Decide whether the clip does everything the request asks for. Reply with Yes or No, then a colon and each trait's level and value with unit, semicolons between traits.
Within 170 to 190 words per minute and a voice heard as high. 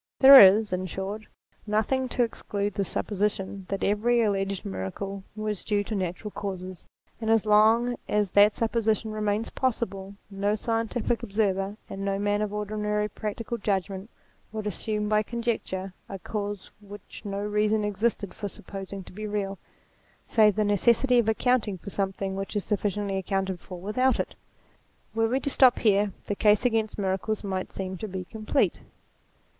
No: average, 160 wpm; high, 210 Hz